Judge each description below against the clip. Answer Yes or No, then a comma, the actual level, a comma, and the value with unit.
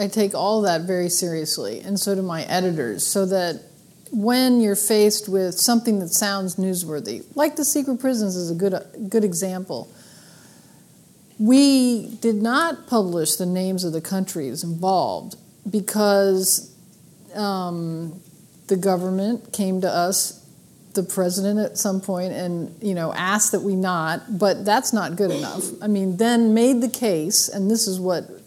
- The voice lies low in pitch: No, high, 195 Hz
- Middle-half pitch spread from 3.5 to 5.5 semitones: No, average, 2.8 semitones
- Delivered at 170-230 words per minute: No, average, 155 wpm